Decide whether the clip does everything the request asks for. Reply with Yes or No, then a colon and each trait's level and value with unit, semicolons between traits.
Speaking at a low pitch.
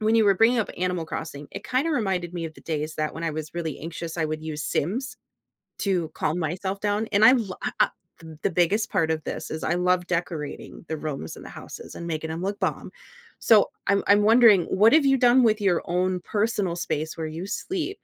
No: medium, 180 Hz